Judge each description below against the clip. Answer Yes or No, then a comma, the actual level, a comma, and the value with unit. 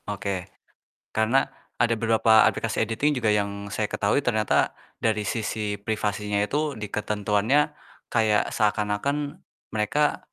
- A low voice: Yes, low, 110 Hz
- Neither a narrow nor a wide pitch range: No, narrow, 2.0 semitones